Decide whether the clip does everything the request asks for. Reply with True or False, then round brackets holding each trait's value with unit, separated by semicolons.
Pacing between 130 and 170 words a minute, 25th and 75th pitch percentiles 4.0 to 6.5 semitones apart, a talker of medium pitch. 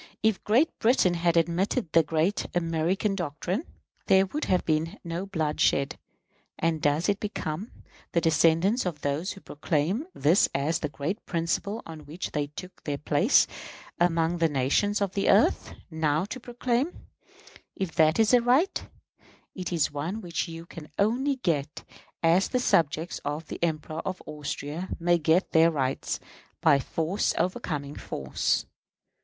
True (155 wpm; 4.3 semitones; 170 Hz)